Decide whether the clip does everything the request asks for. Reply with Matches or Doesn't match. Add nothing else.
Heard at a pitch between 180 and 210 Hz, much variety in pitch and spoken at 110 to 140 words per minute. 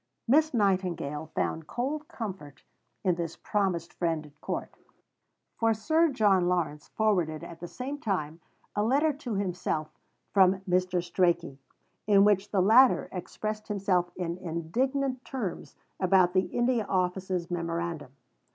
Doesn't match